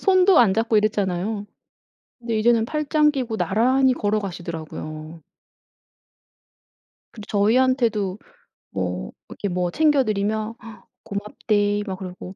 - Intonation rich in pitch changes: No, average, 3.9 semitones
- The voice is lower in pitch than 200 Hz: No, high, 215 Hz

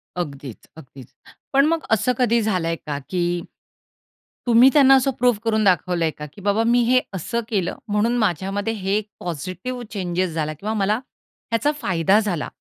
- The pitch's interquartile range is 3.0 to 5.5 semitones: Yes, average, 5.2 semitones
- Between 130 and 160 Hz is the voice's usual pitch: No, high, 200 Hz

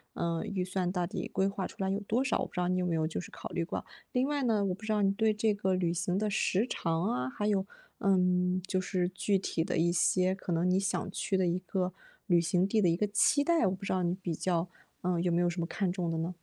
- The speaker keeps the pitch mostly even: Yes, narrow, 2.2 semitones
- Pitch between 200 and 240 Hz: No, medium, 185 Hz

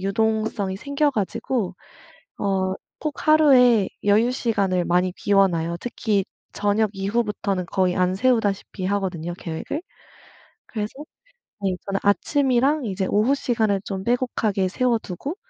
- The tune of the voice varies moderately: Yes, average, 4.1 semitones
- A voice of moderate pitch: No, high, 205 Hz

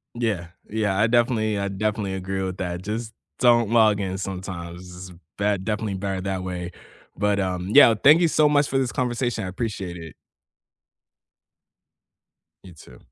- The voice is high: No, low, 100 Hz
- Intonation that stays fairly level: No, average, 3.6 semitones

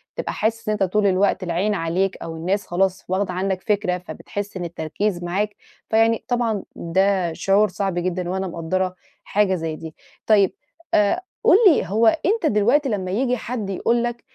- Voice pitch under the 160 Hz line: No, high, 195 Hz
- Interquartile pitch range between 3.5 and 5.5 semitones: No, average, 2.8 semitones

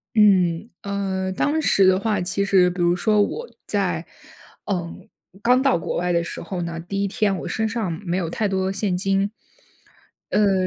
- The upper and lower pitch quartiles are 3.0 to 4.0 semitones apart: No, narrow, 2.6 semitones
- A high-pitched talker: Yes, high, 195 Hz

